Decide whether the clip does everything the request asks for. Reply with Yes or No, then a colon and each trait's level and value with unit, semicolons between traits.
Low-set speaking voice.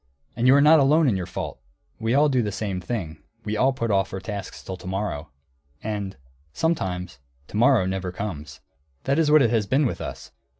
Yes: low, 105 Hz